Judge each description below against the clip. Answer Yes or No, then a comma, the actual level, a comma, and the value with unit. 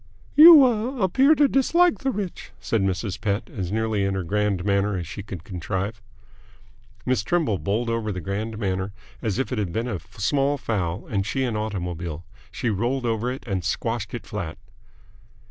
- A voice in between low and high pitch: No, low, 105 Hz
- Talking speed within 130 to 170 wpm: No, average, 180 wpm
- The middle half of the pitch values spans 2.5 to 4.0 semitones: No, average, 4.7 semitones